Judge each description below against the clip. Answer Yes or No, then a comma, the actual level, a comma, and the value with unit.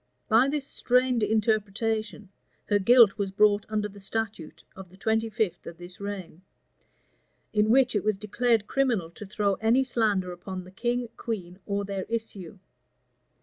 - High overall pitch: Yes, high, 210 Hz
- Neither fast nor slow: Yes, average, 155 wpm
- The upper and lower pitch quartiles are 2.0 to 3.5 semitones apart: Yes, average, 2.8 semitones